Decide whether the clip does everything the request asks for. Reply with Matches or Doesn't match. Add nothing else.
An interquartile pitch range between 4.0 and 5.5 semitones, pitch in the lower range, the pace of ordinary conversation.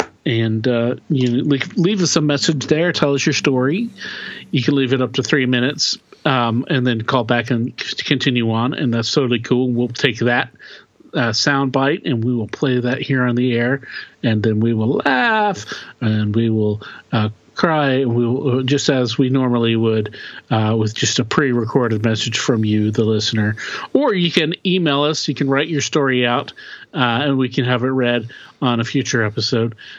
Doesn't match